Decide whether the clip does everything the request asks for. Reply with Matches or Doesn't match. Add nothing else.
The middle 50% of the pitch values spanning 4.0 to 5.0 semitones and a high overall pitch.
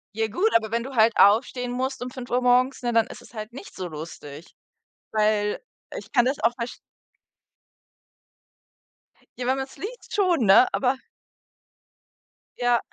Doesn't match